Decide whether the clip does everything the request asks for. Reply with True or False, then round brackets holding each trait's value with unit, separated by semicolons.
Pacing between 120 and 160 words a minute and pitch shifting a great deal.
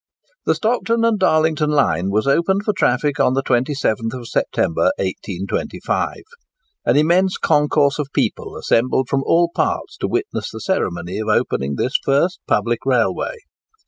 True (145 wpm; 7.0 semitones)